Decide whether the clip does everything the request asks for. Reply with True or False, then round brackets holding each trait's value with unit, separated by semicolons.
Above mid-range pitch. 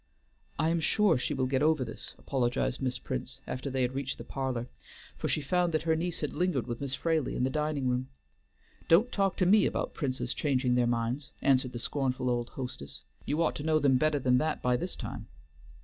False (135 Hz)